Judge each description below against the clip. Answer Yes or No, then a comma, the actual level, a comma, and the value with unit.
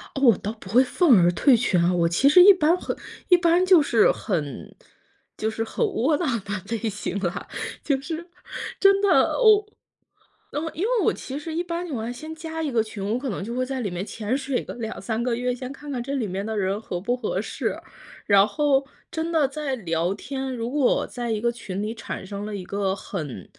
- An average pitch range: No, wide, 6.6 semitones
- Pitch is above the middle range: Yes, high, 245 Hz